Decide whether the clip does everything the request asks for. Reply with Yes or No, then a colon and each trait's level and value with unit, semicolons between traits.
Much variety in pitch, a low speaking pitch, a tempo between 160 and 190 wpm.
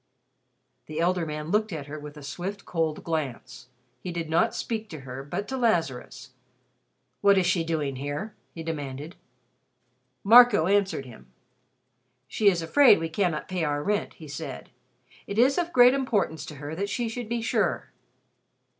No: wide, 5.7 semitones; medium, 170 Hz; average, 165 wpm